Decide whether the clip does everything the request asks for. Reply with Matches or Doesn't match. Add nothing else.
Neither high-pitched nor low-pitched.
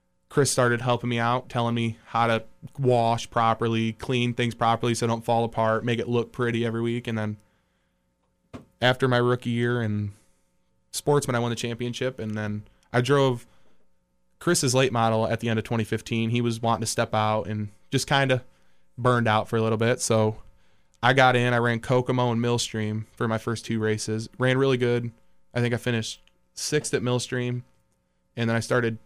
Doesn't match